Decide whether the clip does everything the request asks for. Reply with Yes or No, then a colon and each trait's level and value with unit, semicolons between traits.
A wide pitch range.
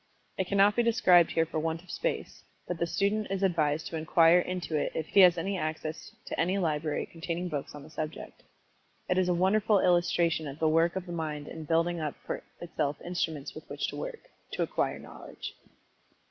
No: average, 2.8 semitones